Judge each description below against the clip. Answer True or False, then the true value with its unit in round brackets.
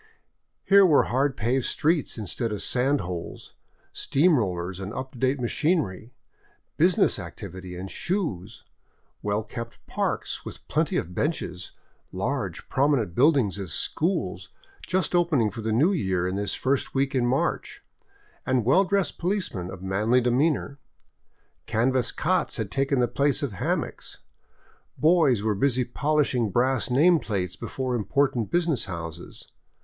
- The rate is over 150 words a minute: False (145 wpm)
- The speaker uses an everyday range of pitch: False (6.2 semitones)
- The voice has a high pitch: False (125 Hz)